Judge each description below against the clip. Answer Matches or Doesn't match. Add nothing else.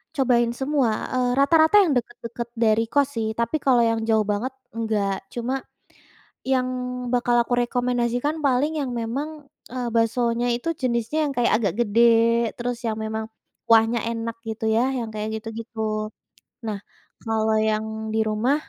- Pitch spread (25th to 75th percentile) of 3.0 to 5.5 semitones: Doesn't match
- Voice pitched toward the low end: Doesn't match